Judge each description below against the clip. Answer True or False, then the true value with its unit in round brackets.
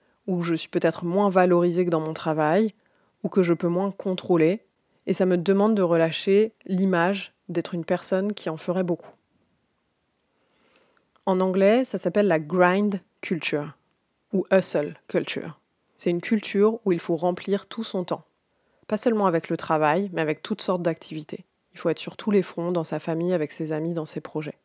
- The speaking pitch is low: False (180 Hz)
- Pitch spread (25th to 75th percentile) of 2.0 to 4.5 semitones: True (2.9 semitones)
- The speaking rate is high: False (185 wpm)